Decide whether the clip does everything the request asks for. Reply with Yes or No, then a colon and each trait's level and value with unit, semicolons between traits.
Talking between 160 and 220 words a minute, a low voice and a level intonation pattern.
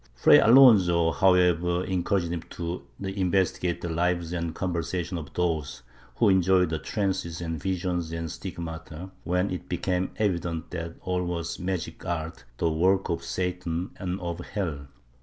No: average, 145 wpm; very low, 90 Hz; narrow, 1.8 semitones